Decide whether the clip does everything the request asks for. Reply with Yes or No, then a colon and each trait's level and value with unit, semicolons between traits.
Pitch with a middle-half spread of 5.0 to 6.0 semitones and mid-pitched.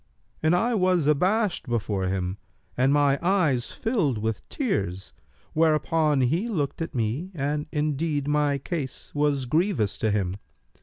Yes: wide, 5.6 semitones; medium, 145 Hz